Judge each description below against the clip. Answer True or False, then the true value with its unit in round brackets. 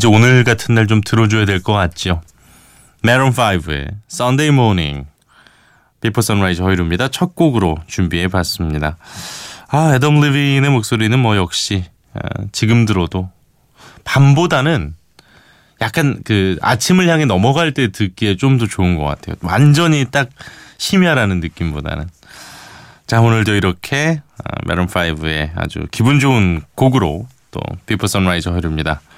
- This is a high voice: False (110 Hz)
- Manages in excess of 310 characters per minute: True (325 characters per minute)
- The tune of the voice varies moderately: False (6.7 semitones)